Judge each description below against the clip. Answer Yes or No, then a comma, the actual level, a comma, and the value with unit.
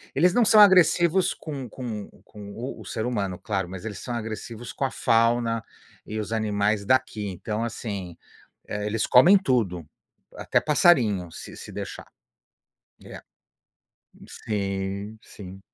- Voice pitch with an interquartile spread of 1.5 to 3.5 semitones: No, average, 4.2 semitones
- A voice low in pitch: Yes, low, 110 Hz